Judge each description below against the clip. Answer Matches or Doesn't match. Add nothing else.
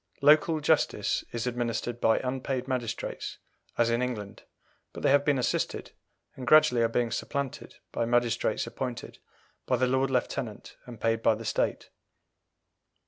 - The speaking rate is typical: Matches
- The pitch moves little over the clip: Matches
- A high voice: Doesn't match